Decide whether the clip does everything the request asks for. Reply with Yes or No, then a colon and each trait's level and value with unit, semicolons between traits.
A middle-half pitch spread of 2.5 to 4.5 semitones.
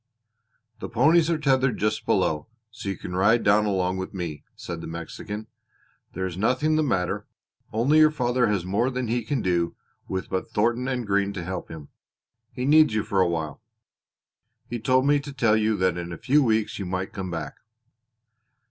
No: wide, 5.6 semitones